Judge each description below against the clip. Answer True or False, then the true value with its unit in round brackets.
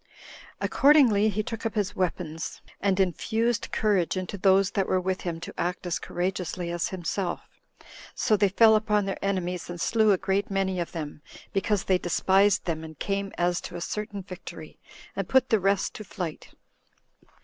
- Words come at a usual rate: True (175 wpm)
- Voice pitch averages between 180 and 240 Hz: True (190 Hz)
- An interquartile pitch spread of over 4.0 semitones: False (2.7 semitones)